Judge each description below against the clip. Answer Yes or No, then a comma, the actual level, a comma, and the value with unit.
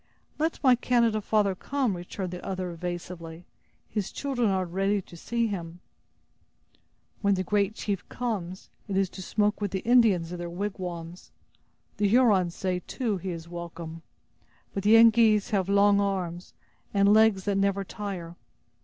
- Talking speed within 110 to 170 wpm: Yes, average, 155 wpm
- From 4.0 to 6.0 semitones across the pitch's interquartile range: No, average, 3.1 semitones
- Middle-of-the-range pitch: No, high, 195 Hz